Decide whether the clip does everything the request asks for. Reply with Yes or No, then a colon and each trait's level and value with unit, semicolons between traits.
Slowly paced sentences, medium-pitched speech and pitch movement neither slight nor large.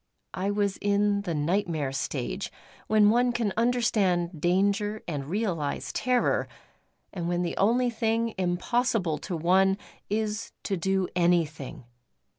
No: slow, 125 wpm; high, 195 Hz; average, 4.0 semitones